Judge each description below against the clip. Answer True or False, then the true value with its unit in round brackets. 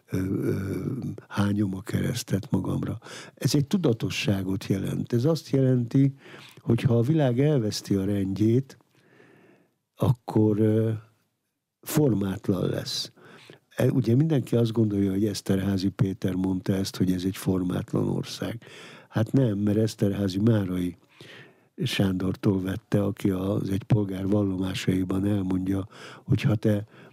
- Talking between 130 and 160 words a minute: False (110 wpm)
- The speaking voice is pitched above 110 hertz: False (105 Hz)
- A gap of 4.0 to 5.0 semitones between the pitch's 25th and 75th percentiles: True (4.5 semitones)